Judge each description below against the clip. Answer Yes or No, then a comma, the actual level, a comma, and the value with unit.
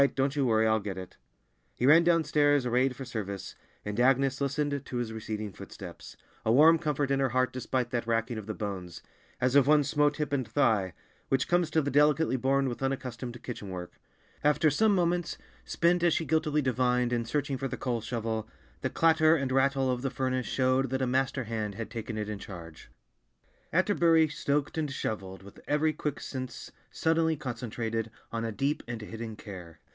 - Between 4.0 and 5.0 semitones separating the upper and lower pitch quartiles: Yes, average, 4.5 semitones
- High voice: No, low, 130 Hz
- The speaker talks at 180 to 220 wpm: Yes, average, 185 wpm